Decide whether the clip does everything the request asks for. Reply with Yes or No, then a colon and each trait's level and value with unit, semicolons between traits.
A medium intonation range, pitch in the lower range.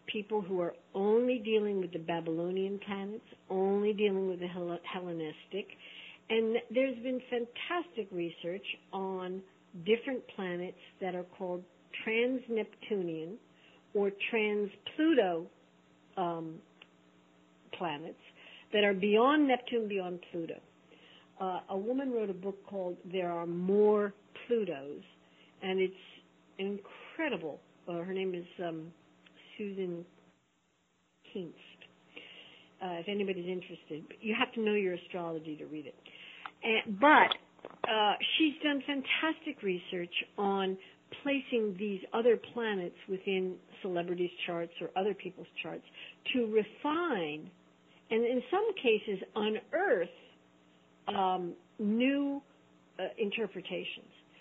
No: average, 4.4 semitones; high, 190 Hz